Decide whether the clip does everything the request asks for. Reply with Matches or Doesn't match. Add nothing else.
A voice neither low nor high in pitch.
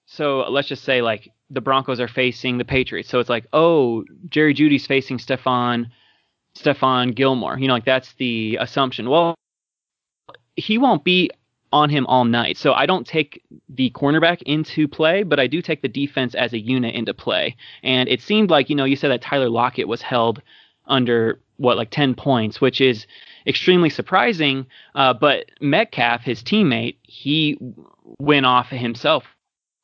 Doesn't match